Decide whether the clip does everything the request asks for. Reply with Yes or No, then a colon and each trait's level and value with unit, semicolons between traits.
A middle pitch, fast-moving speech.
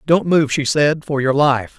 Yes: medium, 145 Hz; fast, 235 wpm